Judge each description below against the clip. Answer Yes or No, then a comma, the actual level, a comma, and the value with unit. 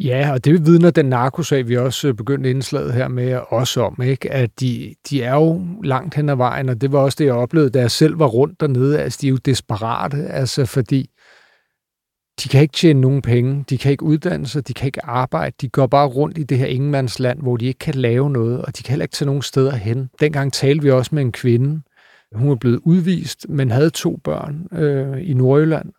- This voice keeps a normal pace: No, fast, 230 wpm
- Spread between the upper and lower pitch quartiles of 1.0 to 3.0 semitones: Yes, narrow, 2.6 semitones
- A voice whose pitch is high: No, low, 135 Hz